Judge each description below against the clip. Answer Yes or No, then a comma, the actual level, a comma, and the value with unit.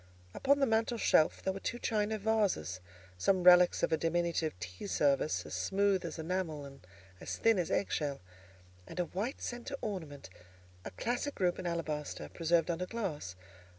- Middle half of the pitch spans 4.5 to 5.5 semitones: Yes, average, 5.2 semitones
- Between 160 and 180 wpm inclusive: Yes, average, 170 wpm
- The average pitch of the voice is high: No, medium, 180 Hz